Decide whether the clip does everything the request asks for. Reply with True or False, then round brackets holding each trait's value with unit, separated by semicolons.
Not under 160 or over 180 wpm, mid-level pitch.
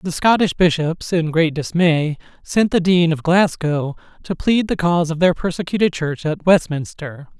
True (170 wpm; 165 Hz)